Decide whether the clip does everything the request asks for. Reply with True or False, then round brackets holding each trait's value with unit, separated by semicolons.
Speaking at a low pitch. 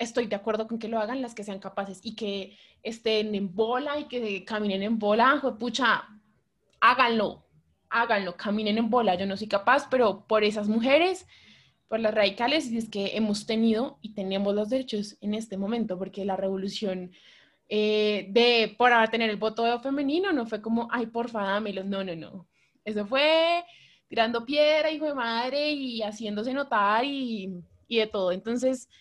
False (220 Hz)